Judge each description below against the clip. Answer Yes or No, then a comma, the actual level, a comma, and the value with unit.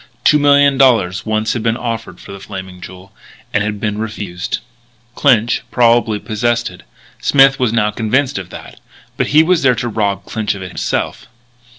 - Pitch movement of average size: Yes, average, 4.0 semitones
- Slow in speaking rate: No, average, 180 wpm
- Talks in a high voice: No, low, 110 Hz